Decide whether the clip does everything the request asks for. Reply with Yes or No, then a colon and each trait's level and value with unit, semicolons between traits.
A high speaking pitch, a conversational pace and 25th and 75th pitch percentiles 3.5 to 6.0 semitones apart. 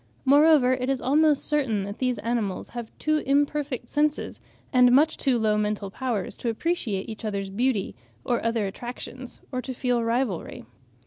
Yes: high, 245 Hz; average, 165 wpm; average, 4.0 semitones